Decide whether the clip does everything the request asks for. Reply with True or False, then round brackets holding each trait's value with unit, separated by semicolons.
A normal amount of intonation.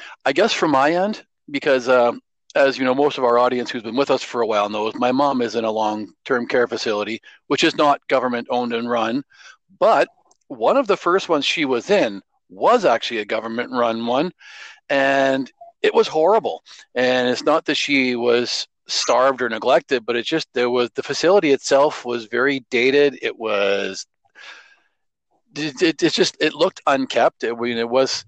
True (3.3 semitones)